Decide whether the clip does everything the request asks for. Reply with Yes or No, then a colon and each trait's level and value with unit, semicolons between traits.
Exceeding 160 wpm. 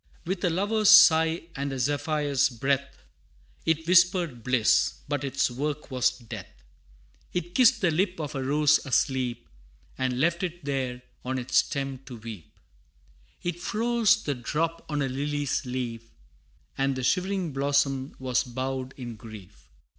No: average, 145 wpm